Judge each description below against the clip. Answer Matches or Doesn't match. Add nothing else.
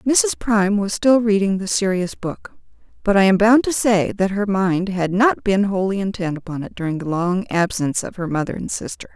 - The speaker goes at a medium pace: Doesn't match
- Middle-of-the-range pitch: Doesn't match